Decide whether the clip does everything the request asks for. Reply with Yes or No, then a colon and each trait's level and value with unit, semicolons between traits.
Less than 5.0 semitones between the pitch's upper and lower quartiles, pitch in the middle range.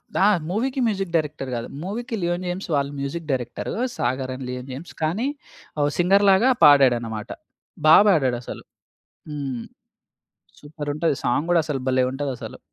No: average, 5.3 semitones; medium, 150 Hz